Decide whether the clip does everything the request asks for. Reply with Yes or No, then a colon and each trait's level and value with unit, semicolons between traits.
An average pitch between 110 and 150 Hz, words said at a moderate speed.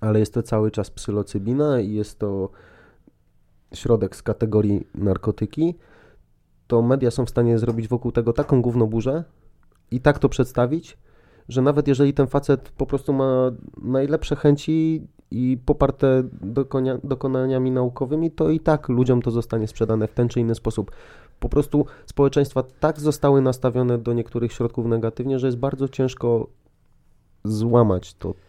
Yes: low, 125 Hz; average, 145 wpm